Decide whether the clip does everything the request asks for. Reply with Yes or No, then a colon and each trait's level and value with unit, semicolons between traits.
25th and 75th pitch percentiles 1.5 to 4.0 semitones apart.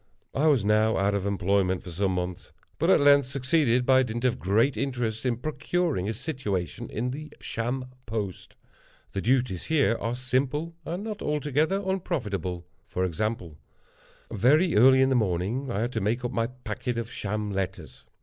No: average, 5.2 semitones